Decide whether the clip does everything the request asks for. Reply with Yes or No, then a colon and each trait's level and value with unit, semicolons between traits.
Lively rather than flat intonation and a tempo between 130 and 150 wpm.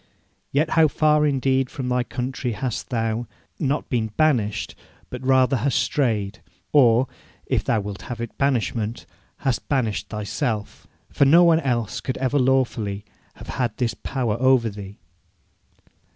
No: average, 3.2 semitones; average, 145 wpm